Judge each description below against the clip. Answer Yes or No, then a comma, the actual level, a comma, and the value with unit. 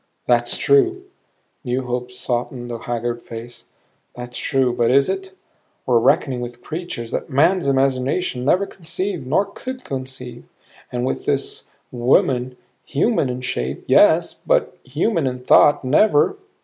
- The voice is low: Yes, low, 130 Hz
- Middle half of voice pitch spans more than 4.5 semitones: Yes, wide, 5.6 semitones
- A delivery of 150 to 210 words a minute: No, slow, 135 wpm